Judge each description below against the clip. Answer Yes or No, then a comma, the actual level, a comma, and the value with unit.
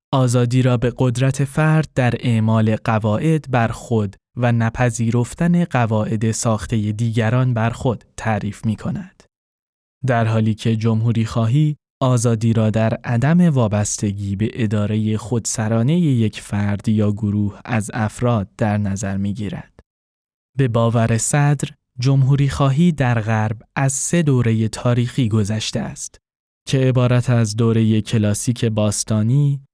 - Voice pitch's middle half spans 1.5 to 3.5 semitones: Yes, average, 2.9 semitones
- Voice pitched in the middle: No, low, 115 Hz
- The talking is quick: No, average, 125 wpm